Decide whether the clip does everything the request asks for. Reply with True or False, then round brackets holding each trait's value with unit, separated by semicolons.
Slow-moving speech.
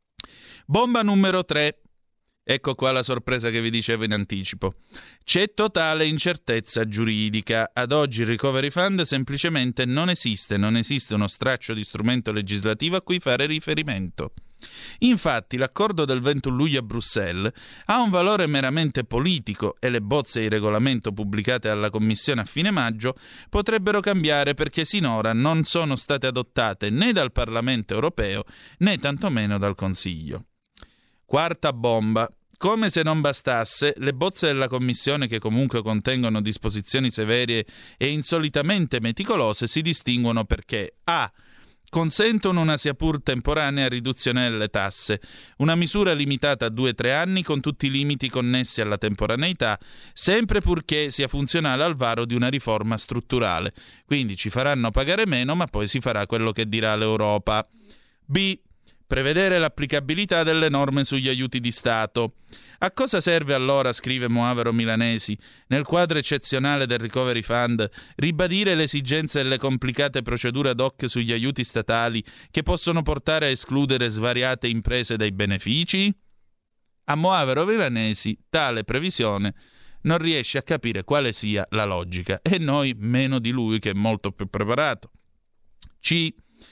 False (145 wpm)